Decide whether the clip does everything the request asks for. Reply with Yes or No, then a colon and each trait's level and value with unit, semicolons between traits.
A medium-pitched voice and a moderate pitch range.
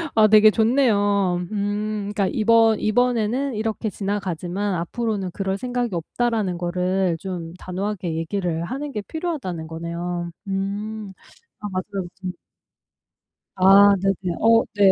No: high, 200 Hz; average, 3.1 semitones